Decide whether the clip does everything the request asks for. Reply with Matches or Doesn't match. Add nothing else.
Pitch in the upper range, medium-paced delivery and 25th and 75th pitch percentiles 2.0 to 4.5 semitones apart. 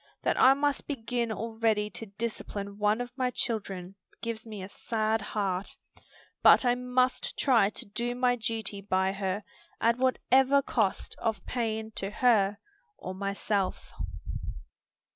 Matches